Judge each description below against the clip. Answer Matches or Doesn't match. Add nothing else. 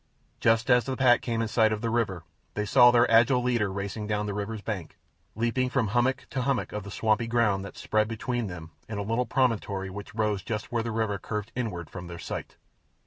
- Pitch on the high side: Doesn't match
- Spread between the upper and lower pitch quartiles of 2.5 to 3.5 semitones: Matches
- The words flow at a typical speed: Doesn't match